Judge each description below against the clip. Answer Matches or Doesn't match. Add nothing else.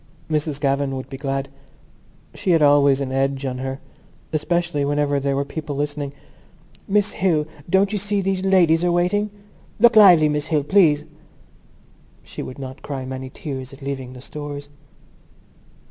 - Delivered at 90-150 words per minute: Doesn't match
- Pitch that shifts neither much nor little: Matches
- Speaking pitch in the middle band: Matches